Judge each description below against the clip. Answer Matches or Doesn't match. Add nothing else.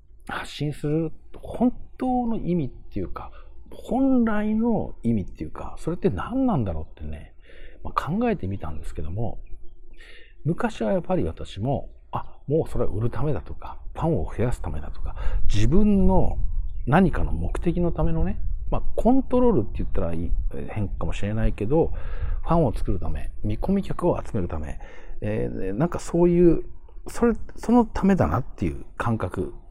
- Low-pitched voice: Matches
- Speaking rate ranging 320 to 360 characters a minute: Matches